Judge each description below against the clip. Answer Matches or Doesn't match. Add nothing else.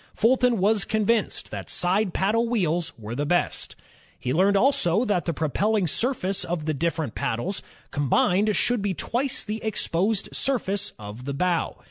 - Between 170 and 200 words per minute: Doesn't match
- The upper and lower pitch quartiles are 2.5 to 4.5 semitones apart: Doesn't match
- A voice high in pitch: Matches